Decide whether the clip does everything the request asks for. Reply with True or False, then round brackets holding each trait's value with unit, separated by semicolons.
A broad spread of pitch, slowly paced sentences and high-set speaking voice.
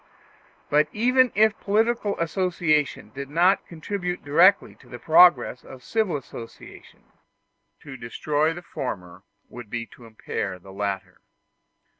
False (7.6 semitones; 125 wpm; 155 Hz)